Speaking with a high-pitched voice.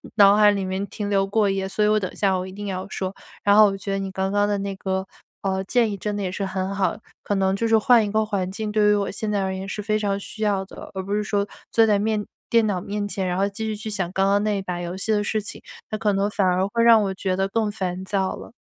Yes: high, 200 Hz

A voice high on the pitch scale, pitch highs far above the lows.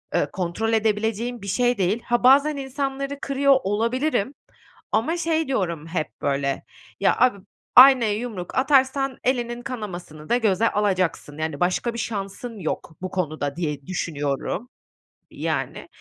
Yes: high, 225 Hz; wide, 6.2 semitones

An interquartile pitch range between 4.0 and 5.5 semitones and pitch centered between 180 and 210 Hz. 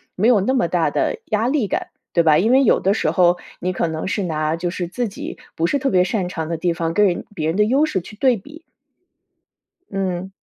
Yes: average, 4.6 semitones; high, 190 Hz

